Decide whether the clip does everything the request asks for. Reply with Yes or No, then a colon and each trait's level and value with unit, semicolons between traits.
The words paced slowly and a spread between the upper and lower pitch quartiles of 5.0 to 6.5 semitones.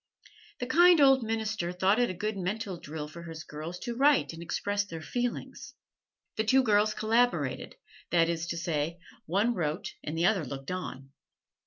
No: average, 175 wpm; wide, 5.6 semitones